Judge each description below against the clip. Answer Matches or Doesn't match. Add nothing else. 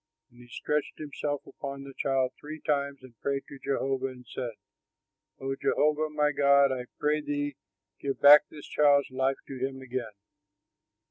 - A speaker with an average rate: Matches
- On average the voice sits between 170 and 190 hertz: Doesn't match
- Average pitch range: Doesn't match